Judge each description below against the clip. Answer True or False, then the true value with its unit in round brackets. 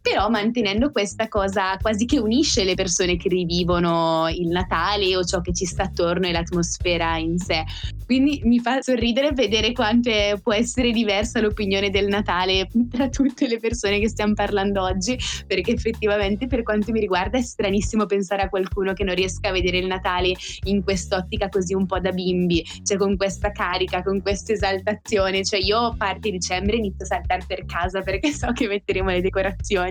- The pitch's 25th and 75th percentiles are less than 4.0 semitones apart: True (3.0 semitones)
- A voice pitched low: False (200 Hz)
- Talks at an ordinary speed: False (185 wpm)